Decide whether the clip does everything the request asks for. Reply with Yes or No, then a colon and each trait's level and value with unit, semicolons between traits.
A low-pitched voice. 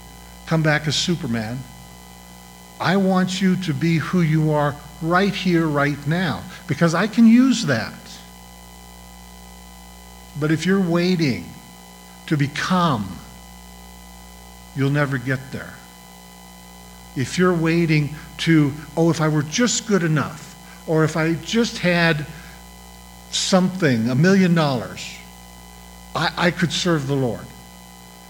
No: medium, 145 Hz